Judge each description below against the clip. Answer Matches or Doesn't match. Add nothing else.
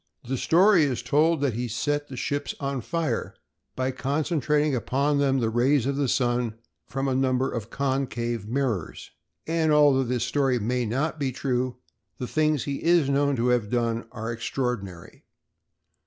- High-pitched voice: Doesn't match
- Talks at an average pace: Matches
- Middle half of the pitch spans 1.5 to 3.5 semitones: Matches